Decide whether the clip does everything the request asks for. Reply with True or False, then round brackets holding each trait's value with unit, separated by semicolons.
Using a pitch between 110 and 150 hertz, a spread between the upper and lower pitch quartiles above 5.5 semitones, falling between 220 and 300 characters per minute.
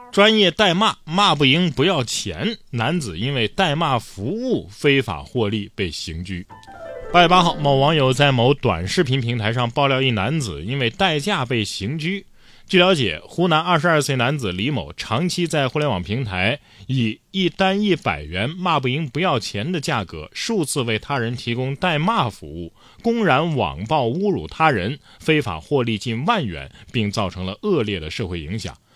True (135 Hz; 7.5 semitones; 260 characters per minute)